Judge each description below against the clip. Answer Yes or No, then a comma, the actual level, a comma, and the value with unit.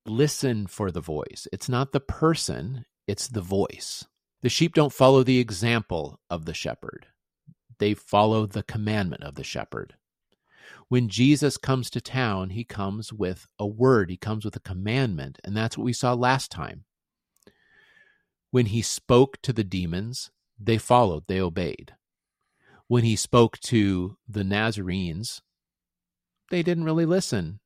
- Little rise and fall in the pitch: No, average, 4.3 semitones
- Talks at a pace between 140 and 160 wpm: Yes, average, 150 wpm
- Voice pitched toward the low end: Yes, low, 115 Hz